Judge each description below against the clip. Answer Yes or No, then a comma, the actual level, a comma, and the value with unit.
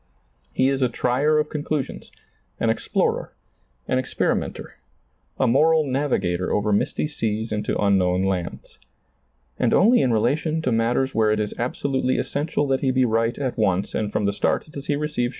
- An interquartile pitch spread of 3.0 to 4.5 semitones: No, average, 5.1 semitones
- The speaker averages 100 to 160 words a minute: No, average, 175 wpm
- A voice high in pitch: No, low, 125 Hz